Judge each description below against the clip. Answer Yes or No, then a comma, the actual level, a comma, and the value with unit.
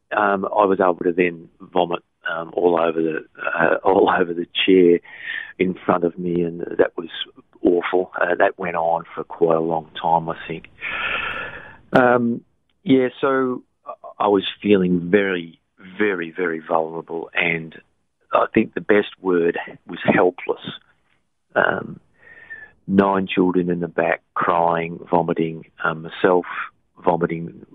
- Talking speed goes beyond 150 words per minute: No, average, 140 wpm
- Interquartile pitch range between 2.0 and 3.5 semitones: Yes, average, 2.9 semitones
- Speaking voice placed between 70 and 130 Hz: Yes, very low, 90 Hz